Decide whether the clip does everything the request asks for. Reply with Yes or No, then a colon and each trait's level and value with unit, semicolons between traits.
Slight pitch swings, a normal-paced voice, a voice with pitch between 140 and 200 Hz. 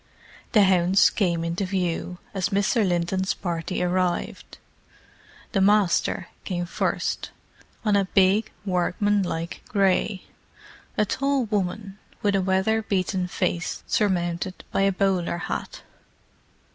No: narrow, 2.2 semitones; slow, 110 wpm; high, 190 Hz